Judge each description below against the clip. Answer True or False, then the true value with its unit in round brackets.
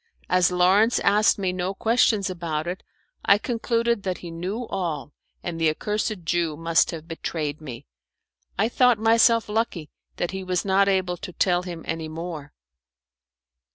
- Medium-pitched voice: True (180 Hz)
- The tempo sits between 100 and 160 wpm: True (155 wpm)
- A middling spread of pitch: True (4.0 semitones)